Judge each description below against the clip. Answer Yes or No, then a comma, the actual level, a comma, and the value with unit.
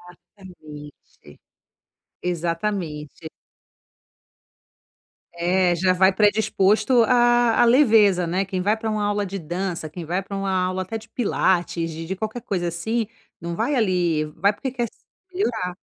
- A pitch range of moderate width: Yes, average, 4.0 semitones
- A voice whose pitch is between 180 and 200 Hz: Yes, high, 190 Hz